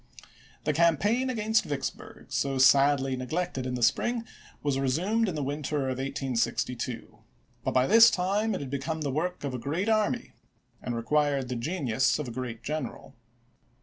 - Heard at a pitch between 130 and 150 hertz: Yes, medium, 140 Hz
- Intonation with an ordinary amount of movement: No, wide, 5.7 semitones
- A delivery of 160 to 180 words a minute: Yes, average, 170 wpm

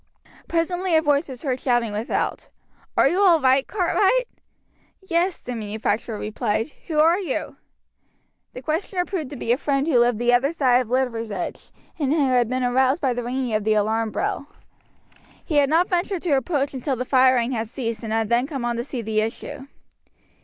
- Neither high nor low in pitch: No, very high, 260 Hz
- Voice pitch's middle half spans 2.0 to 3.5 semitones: No, average, 4.7 semitones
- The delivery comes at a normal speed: Yes, average, 190 wpm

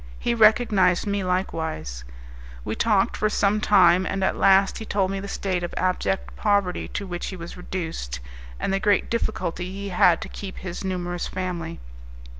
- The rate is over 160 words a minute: Yes, average, 175 wpm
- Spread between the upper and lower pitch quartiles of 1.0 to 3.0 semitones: Yes, narrow, 2.4 semitones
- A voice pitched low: No, medium, 185 Hz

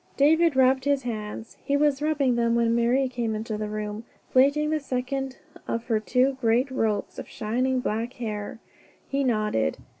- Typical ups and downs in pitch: Yes, average, 3.5 semitones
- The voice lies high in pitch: Yes, very high, 250 Hz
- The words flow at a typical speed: Yes, average, 170 wpm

